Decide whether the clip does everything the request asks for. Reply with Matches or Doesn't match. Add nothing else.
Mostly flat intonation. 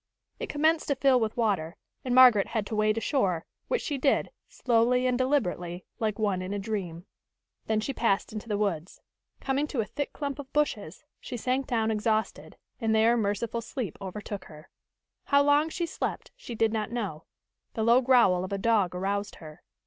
Doesn't match